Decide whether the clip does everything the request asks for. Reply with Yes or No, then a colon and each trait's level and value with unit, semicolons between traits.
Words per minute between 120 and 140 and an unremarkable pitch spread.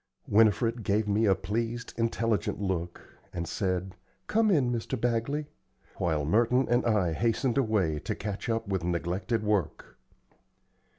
Yes: slow, 135 wpm; average, 3.9 semitones